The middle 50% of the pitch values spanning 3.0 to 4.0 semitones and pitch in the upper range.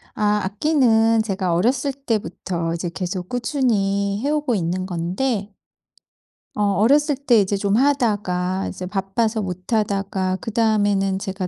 Yes: average, 3.6 semitones; high, 205 Hz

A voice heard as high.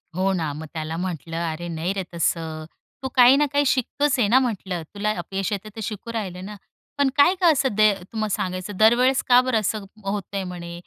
Yes: high, 200 Hz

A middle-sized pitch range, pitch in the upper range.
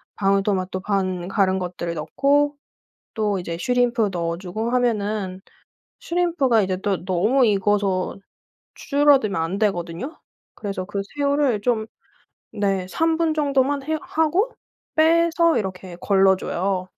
No: wide, 6.8 semitones; high, 205 Hz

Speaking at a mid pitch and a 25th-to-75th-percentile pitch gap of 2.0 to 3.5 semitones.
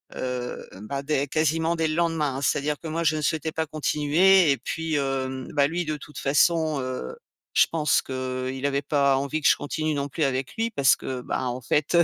Yes: medium, 145 Hz; average, 3.0 semitones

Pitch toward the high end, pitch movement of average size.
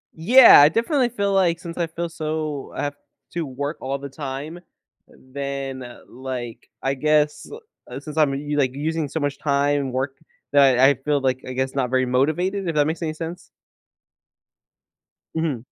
No: medium, 145 Hz; average, 3.3 semitones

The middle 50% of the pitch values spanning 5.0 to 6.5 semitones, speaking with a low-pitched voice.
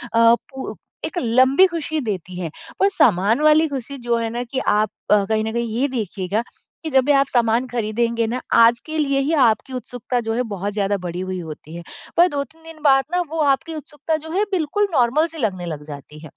No: wide, 5.6 semitones; high, 245 Hz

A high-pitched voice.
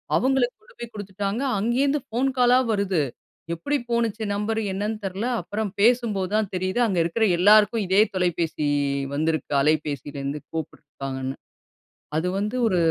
Yes: high, 205 Hz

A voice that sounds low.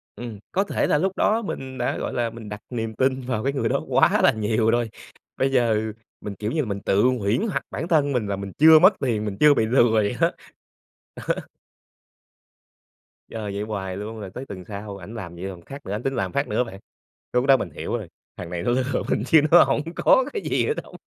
Yes: low, 115 Hz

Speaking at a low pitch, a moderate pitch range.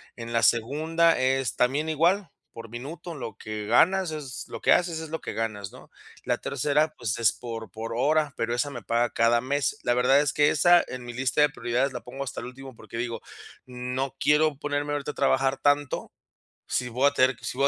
Yes: low, 130 Hz; average, 3.7 semitones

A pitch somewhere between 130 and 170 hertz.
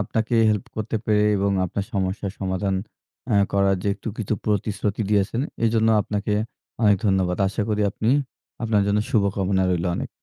No: low, 100 Hz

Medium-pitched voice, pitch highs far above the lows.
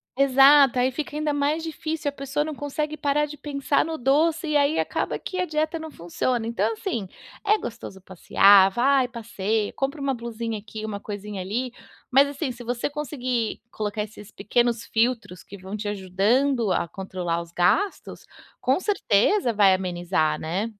No: high, 245 Hz; wide, 6.0 semitones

